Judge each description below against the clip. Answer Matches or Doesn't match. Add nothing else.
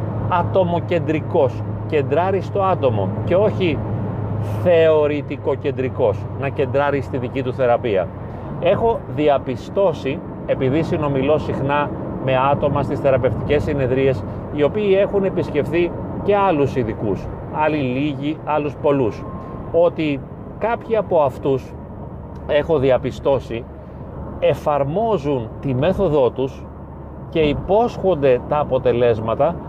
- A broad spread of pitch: Doesn't match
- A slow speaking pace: Matches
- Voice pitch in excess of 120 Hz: Matches